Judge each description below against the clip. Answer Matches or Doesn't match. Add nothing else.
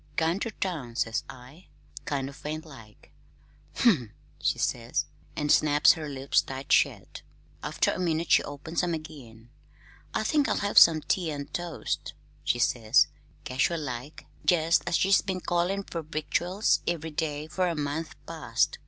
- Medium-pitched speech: Matches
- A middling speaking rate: Matches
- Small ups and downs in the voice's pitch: Doesn't match